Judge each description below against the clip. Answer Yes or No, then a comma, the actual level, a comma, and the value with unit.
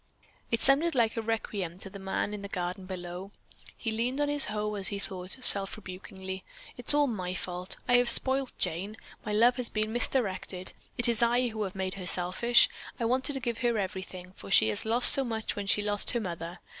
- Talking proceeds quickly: Yes, fast, 220 wpm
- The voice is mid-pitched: No, high, 210 Hz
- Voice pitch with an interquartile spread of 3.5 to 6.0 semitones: Yes, average, 4.2 semitones